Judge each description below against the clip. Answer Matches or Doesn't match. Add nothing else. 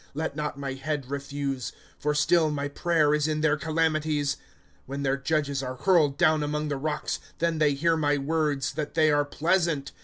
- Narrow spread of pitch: Matches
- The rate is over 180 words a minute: Matches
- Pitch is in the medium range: Matches